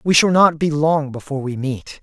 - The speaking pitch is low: No, medium, 150 Hz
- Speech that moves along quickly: Yes, fast, 235 wpm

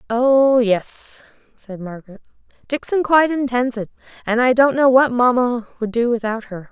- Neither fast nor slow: Yes, average, 160 wpm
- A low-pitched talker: No, high, 240 Hz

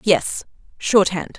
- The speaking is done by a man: No, female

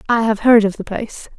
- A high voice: Yes, high, 220 Hz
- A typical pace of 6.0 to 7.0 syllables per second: Yes, 6.1 syllables/s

